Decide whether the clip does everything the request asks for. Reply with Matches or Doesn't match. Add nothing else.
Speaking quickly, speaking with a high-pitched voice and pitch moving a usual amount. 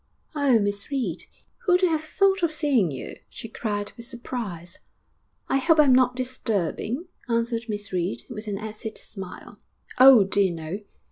Doesn't match